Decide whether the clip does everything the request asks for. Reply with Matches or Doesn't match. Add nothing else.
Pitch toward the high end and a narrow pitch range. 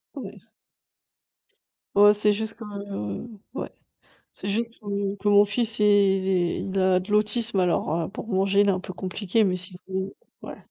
Matches